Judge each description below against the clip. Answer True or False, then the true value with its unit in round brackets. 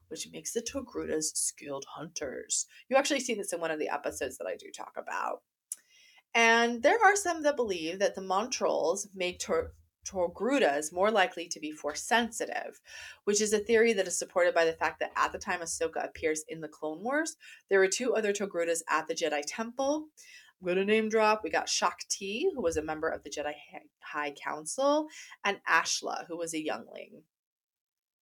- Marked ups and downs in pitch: True (8.1 semitones)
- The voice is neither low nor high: False (195 Hz)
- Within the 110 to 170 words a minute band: False (190 wpm)